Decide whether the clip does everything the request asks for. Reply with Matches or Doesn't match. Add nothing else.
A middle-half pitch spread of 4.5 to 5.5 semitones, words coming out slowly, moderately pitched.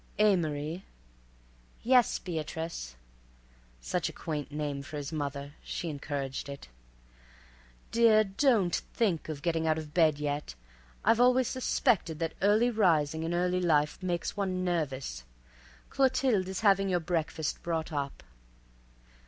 Matches